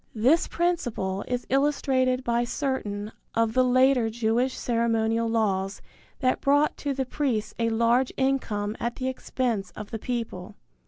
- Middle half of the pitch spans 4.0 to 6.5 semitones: No, average, 2.9 semitones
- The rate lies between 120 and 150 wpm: Yes, average, 145 wpm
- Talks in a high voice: Yes, high, 240 Hz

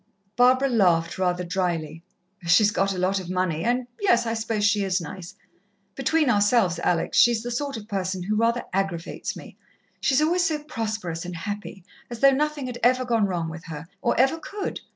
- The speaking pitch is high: Yes, high, 210 Hz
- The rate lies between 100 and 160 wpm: No, average, 190 wpm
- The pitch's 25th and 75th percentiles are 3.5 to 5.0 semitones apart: No, wide, 5.4 semitones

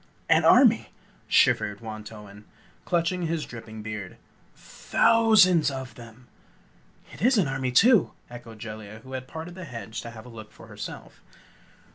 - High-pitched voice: No, low, 120 Hz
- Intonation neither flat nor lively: No, wide, 7.3 semitones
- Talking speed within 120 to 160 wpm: Yes, average, 150 wpm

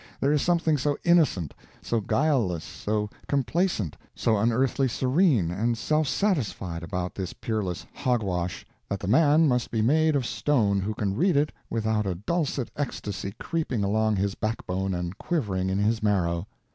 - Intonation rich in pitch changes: Yes, wide, 6.8 semitones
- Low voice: Yes, low, 110 Hz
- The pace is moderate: Yes, average, 160 wpm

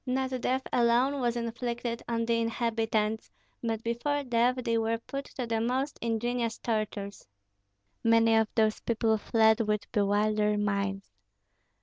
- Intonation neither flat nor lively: No, narrow, 1.6 semitones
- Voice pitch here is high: Yes, high, 230 Hz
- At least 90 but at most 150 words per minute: Yes, slow, 135 wpm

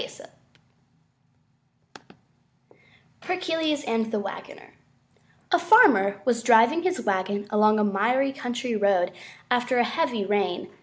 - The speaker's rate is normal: No, slow, 110 wpm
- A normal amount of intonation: No, wide, 6.2 semitones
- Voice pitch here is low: No, high, 235 Hz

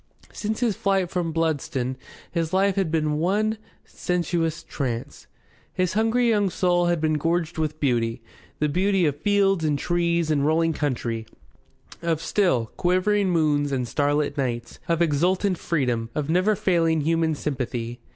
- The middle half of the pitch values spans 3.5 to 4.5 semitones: Yes, average, 4.0 semitones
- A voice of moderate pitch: Yes, medium, 165 Hz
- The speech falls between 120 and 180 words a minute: Yes, average, 150 wpm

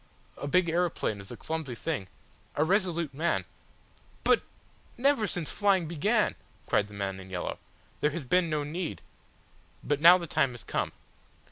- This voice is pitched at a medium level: Yes, medium, 160 Hz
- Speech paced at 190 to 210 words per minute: No, average, 170 wpm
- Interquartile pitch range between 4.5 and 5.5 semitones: Yes, average, 4.8 semitones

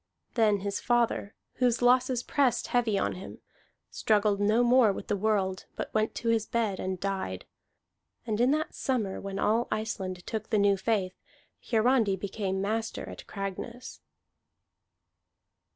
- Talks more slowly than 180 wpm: Yes, average, 150 wpm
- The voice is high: Yes, high, 215 Hz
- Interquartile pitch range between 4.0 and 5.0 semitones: No, average, 3.2 semitones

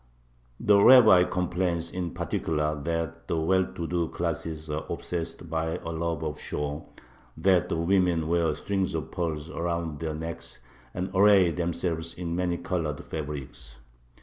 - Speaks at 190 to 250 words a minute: No, average, 150 wpm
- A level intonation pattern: Yes, narrow, 2.0 semitones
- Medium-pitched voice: No, very low, 85 Hz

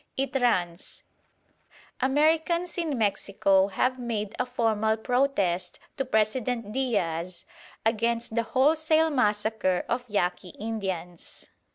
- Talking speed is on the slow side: Yes, slow, 100 wpm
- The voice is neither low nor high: No, high, 225 Hz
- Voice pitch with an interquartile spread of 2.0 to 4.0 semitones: No, average, 4.7 semitones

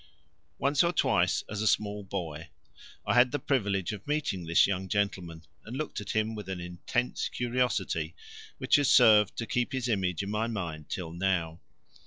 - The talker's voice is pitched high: No, low, 100 Hz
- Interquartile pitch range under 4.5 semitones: No, average, 5.1 semitones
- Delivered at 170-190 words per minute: Yes, average, 180 wpm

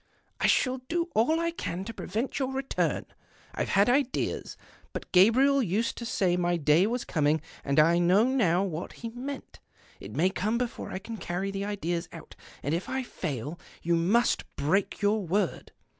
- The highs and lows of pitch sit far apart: Yes, wide, 5.9 semitones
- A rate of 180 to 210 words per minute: Yes, average, 185 wpm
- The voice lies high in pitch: Yes, high, 200 Hz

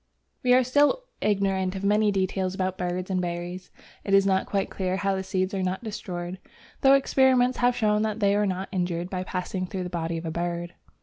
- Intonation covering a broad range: No, narrow, 2.4 semitones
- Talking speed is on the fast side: Yes, fast, 210 wpm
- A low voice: No, high, 190 Hz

